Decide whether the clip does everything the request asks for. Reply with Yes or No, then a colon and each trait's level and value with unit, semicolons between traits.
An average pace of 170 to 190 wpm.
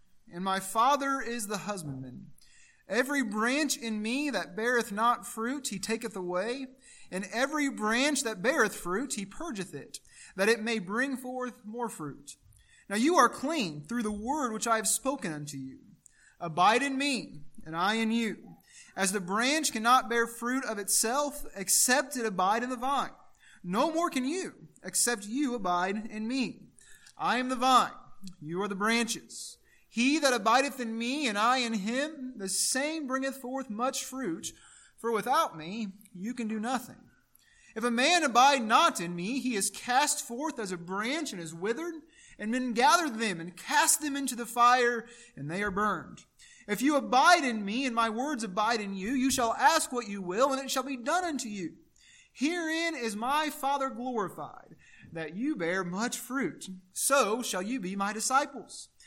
Yes: average, 180 wpm